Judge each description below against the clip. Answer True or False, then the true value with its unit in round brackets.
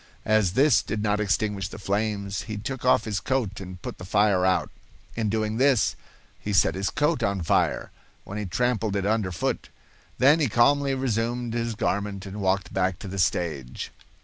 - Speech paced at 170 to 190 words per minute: True (185 wpm)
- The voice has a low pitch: True (105 Hz)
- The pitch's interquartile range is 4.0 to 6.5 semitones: False (3.4 semitones)